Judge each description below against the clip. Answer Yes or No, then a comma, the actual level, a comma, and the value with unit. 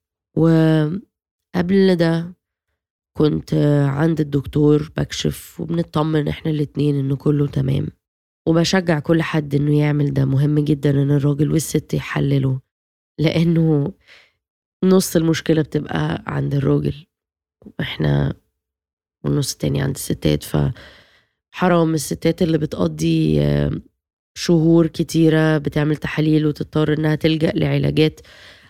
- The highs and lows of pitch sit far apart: No, narrow, 2.5 semitones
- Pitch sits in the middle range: Yes, medium, 150 Hz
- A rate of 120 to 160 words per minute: No, average, 100 wpm